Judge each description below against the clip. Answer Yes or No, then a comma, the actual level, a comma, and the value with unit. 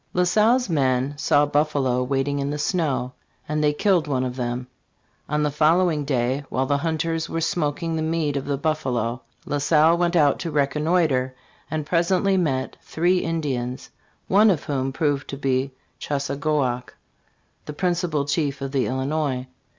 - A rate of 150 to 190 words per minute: Yes, average, 165 wpm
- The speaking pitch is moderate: Yes, medium, 145 Hz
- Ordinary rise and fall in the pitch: Yes, average, 3.5 semitones